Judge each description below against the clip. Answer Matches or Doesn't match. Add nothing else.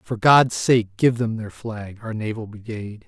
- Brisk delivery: Doesn't match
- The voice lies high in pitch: Doesn't match